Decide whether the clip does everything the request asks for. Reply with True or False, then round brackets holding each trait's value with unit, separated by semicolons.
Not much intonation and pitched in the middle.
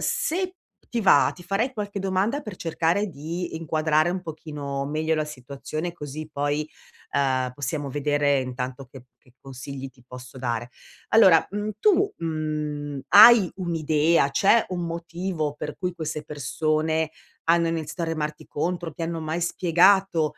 False (3.5 semitones; 160 Hz)